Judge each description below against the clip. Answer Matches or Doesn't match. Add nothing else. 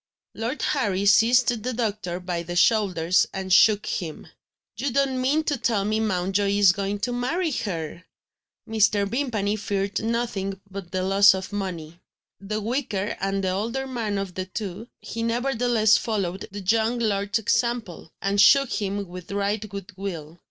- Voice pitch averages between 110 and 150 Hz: Doesn't match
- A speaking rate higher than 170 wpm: Doesn't match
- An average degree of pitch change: Matches